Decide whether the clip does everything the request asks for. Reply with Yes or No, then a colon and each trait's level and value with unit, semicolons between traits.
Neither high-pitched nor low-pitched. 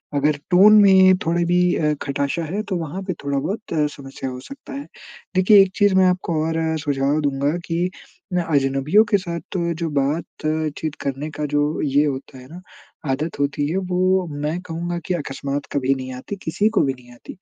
Yes: medium, 155 Hz